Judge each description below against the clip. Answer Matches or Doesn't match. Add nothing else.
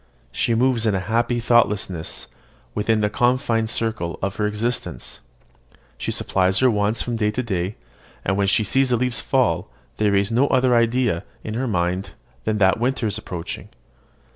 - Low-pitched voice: Matches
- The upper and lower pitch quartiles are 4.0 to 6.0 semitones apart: Doesn't match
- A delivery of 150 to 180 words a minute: Matches